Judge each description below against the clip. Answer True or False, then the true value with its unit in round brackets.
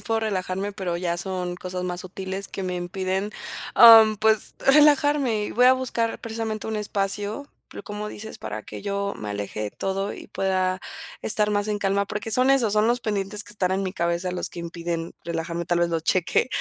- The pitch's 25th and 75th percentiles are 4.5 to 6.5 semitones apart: False (3.1 semitones)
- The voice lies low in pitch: False (195 Hz)